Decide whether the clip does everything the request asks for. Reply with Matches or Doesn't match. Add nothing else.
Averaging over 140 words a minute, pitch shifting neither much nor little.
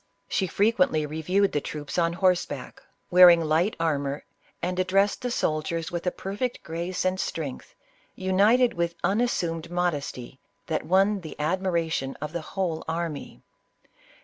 Doesn't match